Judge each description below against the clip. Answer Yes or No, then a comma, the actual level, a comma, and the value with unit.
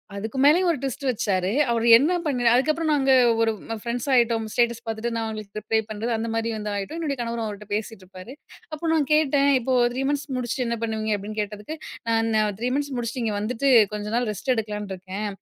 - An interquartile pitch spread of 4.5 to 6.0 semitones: No, average, 4.0 semitones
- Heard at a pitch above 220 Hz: Yes, high, 230 Hz